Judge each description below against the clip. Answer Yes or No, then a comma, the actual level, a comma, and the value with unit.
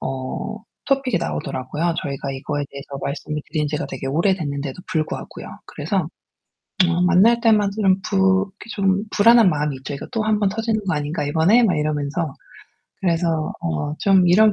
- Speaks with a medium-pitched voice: Yes, medium, 170 Hz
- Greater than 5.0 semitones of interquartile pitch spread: Yes, wide, 5.6 semitones